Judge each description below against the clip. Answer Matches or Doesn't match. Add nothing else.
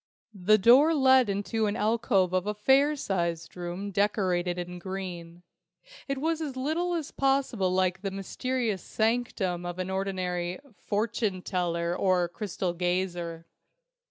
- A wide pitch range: Doesn't match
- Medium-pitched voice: Doesn't match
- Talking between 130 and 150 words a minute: Matches